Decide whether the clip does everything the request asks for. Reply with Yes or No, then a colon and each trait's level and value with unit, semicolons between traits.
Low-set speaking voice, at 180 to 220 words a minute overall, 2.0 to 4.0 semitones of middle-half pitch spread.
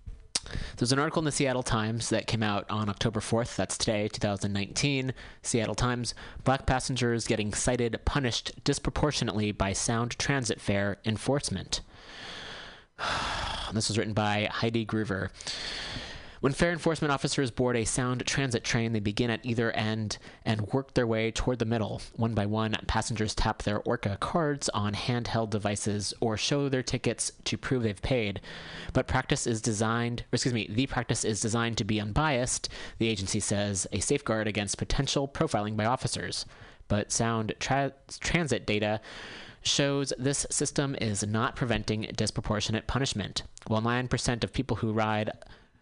No: low, 115 Hz; average, 155 wpm; average, 3.3 semitones